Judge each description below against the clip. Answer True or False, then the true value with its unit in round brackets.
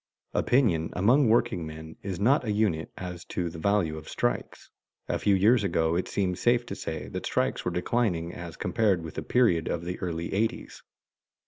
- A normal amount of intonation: True (5.0 semitones)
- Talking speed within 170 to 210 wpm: True (185 wpm)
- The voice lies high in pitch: False (90 Hz)